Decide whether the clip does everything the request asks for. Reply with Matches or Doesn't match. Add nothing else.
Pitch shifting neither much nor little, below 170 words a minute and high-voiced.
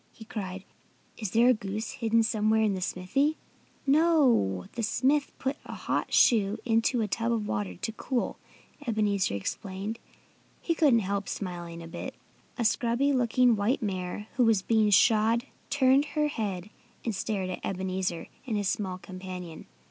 Matches